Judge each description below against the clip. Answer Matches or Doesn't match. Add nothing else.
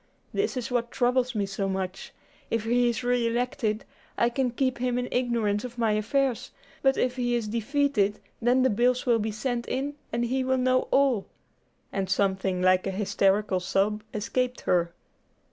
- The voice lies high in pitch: Matches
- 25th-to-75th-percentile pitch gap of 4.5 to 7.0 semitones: Doesn't match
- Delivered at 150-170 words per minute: Doesn't match